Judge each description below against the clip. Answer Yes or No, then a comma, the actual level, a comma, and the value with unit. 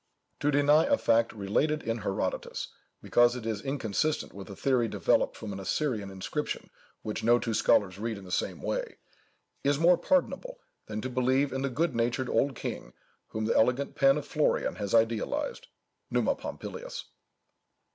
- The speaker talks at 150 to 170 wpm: Yes, average, 165 wpm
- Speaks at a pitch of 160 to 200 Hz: No, low, 120 Hz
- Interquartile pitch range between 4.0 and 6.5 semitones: Yes, average, 5.0 semitones